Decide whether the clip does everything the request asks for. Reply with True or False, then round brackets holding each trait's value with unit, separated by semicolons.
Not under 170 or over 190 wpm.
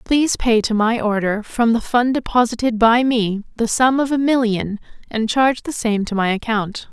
False (200 wpm)